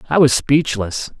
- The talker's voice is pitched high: No, low, 130 Hz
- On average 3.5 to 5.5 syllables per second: Yes, 4.1 syllables/s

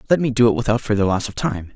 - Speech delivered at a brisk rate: Yes, fast, 305 wpm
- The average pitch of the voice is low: Yes, low, 115 Hz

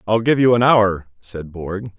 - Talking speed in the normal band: No, fast, 210 wpm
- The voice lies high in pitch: No, low, 100 Hz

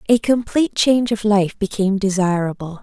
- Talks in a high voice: Yes, high, 205 Hz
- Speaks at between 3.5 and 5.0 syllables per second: No, 5.8 syllables/s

